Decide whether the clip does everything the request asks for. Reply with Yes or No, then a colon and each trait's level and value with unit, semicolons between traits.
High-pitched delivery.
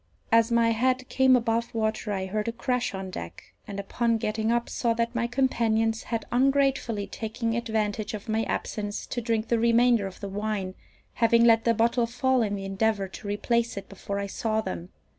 Yes: high, 225 Hz